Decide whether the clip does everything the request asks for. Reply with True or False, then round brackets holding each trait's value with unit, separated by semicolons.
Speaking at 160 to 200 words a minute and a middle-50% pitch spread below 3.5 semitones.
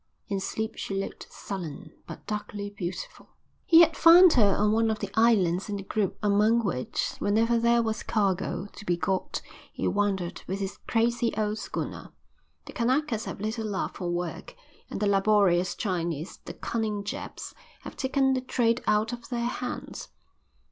True (170 wpm; 3.1 semitones)